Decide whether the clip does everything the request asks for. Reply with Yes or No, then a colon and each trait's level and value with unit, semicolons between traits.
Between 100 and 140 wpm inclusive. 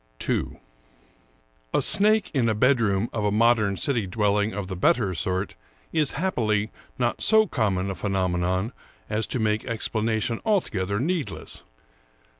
Yes: slow, 135 wpm